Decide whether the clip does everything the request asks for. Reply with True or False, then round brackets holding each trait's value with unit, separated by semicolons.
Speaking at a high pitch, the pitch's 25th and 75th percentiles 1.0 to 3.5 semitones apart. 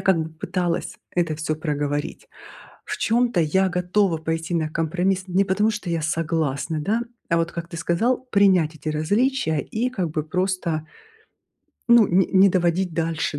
False (170 Hz; 3.2 semitones)